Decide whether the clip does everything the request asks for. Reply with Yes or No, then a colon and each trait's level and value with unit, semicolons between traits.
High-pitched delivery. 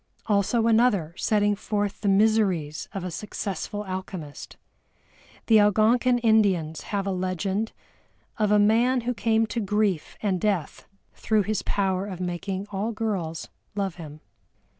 Yes: high, 205 Hz